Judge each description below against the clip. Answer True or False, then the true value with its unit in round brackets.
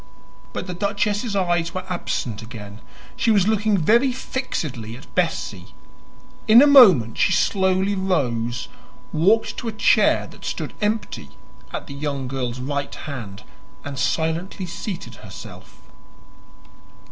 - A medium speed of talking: False (130 wpm)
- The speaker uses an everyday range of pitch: False (8.0 semitones)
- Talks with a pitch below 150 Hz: False (175 Hz)